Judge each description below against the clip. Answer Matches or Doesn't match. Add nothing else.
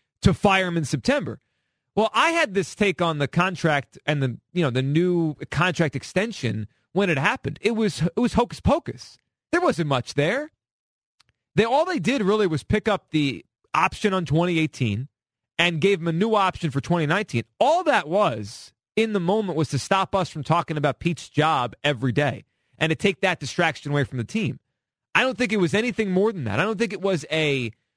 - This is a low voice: Doesn't match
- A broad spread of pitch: Matches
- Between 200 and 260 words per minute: Matches